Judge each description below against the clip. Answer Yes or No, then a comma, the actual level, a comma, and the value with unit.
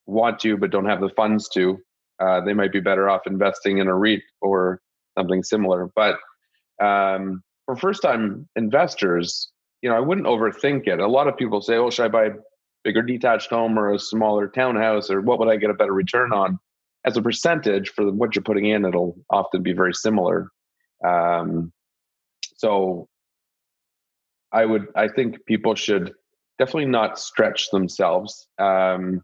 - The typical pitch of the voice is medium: No, low, 100 Hz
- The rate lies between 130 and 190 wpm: Yes, average, 175 wpm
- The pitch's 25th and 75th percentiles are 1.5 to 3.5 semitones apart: Yes, average, 3.0 semitones